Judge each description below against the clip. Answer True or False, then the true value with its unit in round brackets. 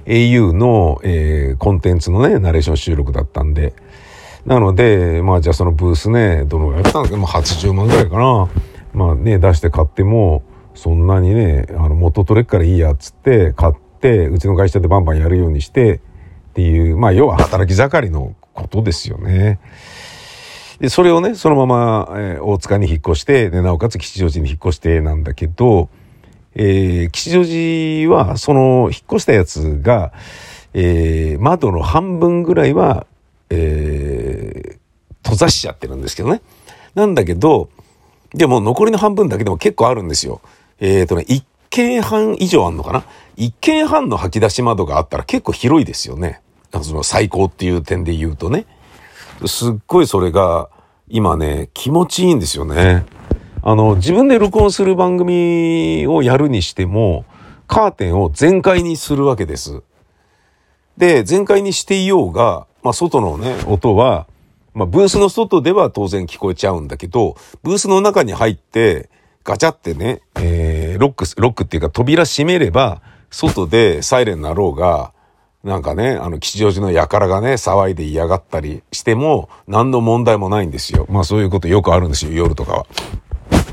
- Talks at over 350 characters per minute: False (340 characters per minute)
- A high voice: False (100 Hz)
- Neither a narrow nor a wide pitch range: False (6.9 semitones)